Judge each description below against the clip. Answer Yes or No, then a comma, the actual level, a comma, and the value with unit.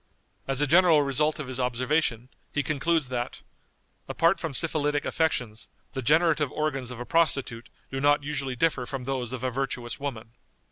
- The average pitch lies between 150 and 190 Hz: No, low, 135 Hz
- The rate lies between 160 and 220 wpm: Yes, average, 170 wpm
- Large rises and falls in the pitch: No, average, 3.4 semitones